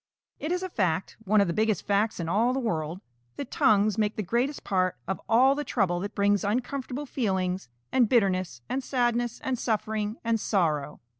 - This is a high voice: Yes, high, 215 Hz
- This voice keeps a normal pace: Yes, average, 195 wpm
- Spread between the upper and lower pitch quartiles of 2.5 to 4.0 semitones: No, average, 4.5 semitones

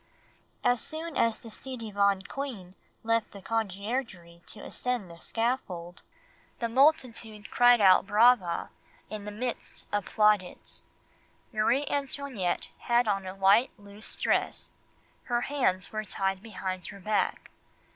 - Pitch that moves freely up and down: No, average, 4.0 semitones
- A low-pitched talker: No, high, 215 Hz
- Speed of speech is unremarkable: No, slow, 130 wpm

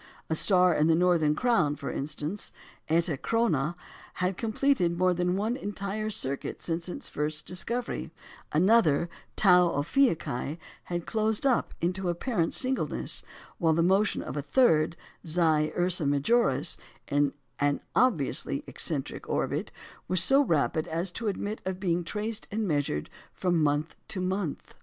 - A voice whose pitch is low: No, medium, 175 Hz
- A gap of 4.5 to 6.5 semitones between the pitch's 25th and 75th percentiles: Yes, average, 5.0 semitones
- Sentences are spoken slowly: No, average, 145 wpm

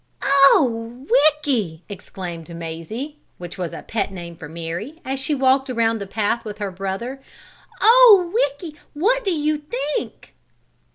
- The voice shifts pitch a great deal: Yes, wide, 7.5 semitones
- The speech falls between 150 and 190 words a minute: No, average, 140 wpm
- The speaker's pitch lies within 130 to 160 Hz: No, high, 245 Hz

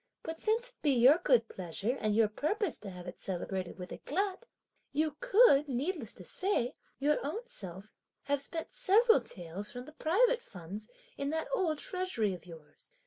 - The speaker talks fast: No, average, 175 wpm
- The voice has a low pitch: No, very high, 280 Hz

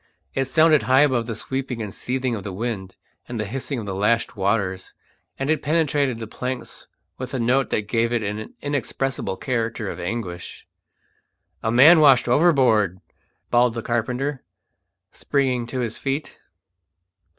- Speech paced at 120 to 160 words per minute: Yes, average, 155 wpm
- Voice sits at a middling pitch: No, low, 120 Hz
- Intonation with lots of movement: No, average, 3.3 semitones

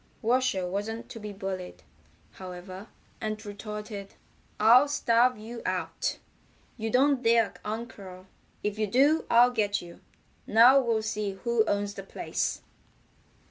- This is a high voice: Yes, high, 215 Hz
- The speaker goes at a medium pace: No, slow, 130 wpm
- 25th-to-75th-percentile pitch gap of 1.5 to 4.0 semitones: Yes, average, 2.8 semitones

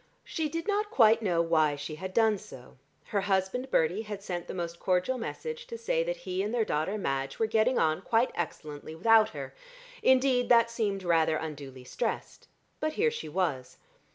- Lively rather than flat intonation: Yes, wide, 7.1 semitones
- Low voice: No, high, 200 Hz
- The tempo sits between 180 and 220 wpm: Yes, average, 185 wpm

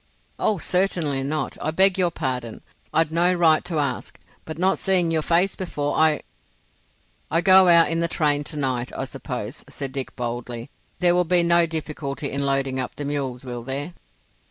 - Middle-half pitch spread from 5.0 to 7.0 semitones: No, average, 4.2 semitones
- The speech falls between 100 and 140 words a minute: No, average, 180 wpm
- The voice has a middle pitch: Yes, medium, 155 Hz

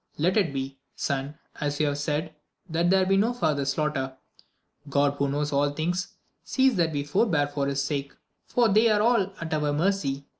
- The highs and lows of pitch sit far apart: No, average, 4.8 semitones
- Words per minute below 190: No, average, 200 wpm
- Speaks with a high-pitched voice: No, medium, 150 Hz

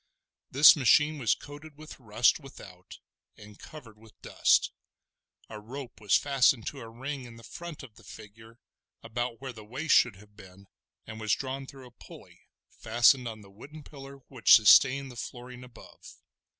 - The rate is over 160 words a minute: Yes, average, 170 wpm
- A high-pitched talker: No, low, 125 Hz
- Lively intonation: No, average, 3.8 semitones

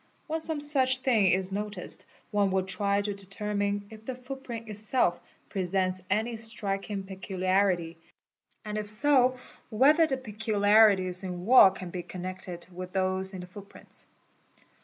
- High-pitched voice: Yes, high, 205 Hz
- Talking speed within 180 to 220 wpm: No, average, 145 wpm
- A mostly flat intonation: No, average, 3.2 semitones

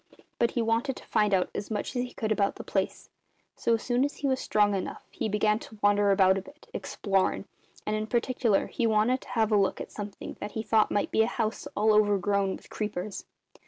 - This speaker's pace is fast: Yes, fast, 230 wpm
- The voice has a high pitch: Yes, high, 215 Hz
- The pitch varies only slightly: Yes, narrow, 2.0 semitones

